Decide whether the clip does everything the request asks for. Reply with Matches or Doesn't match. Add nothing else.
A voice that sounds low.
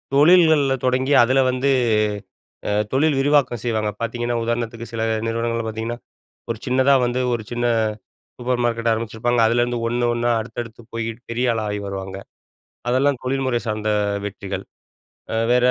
Matches